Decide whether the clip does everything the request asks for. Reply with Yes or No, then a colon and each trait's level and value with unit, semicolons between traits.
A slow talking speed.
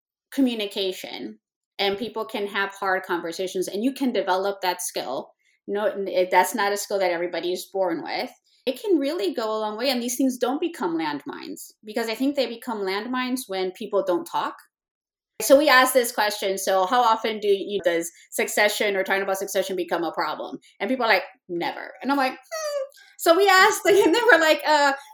No: fast, 205 wpm